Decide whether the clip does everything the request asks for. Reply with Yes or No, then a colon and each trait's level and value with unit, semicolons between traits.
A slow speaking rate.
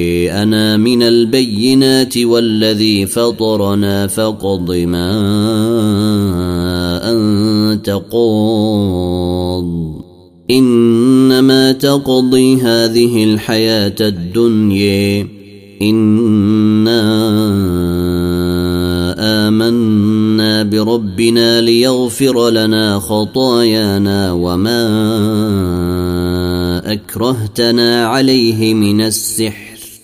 Yes: slow, 50 wpm